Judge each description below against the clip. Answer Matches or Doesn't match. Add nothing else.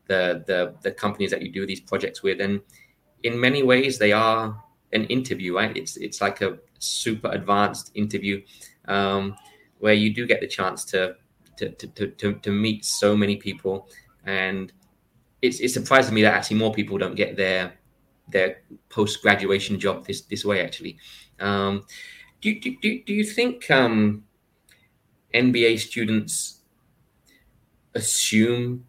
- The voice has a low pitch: Matches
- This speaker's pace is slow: Doesn't match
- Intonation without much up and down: Doesn't match